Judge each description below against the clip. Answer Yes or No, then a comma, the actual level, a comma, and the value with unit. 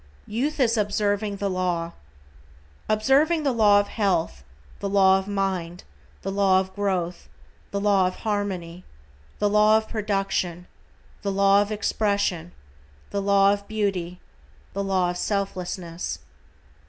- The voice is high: Yes, high, 200 Hz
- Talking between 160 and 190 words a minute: No, slow, 135 wpm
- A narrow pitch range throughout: Yes, narrow, 2.1 semitones